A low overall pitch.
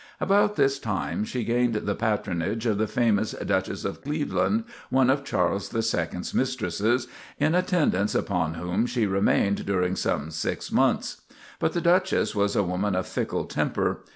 Yes: low, 110 Hz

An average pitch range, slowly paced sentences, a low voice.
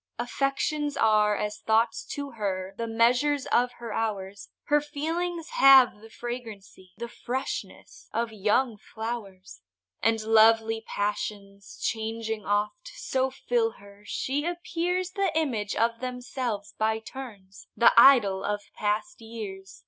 No: average, 4.1 semitones; slow, 125 wpm; high, 225 Hz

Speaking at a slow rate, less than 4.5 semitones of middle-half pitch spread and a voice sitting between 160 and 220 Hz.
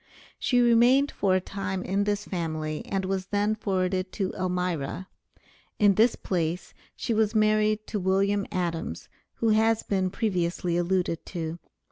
No: average, 145 wpm; average, 2.9 semitones; high, 190 Hz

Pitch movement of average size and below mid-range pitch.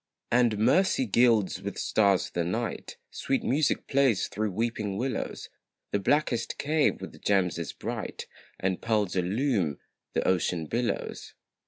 Yes: average, 4.6 semitones; low, 110 Hz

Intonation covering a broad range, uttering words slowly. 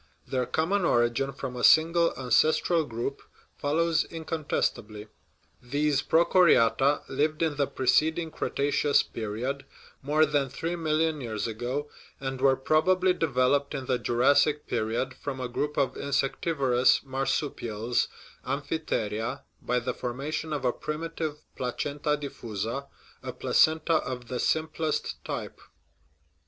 No: average, 3.8 semitones; slow, 120 wpm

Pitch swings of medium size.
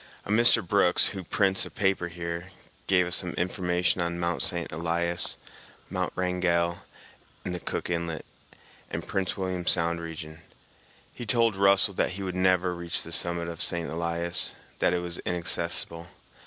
No: narrow, 1.5 semitones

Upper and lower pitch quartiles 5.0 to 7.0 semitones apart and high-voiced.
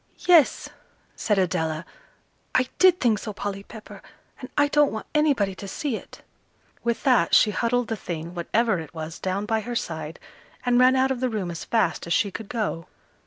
Yes: average, 5.3 semitones; high, 215 Hz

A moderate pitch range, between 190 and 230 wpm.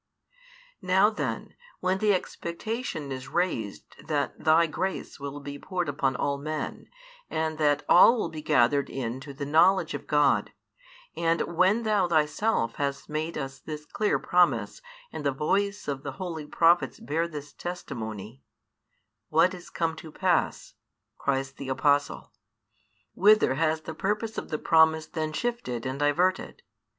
No: average, 4.2 semitones; average, 150 wpm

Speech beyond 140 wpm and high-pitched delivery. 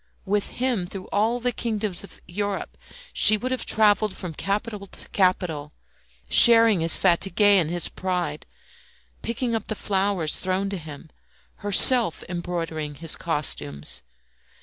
No: slow, 135 wpm; high, 195 Hz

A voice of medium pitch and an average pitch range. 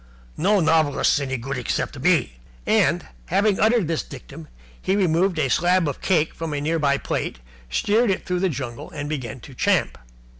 Yes: medium, 155 Hz; average, 4.9 semitones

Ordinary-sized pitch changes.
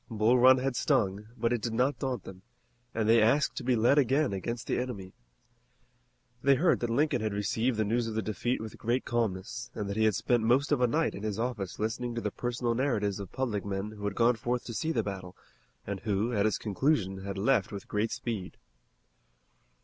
Yes: average, 3.3 semitones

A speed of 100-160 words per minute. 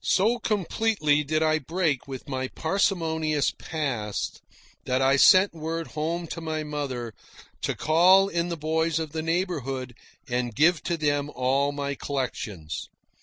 Yes: average, 145 wpm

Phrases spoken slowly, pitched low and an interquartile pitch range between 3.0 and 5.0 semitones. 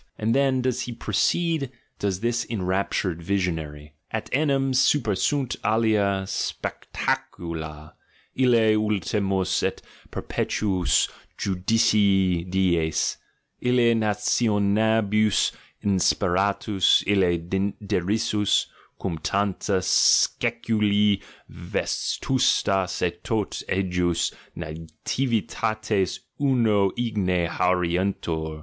Yes: slow, 80 wpm; low, 100 Hz; average, 3.6 semitones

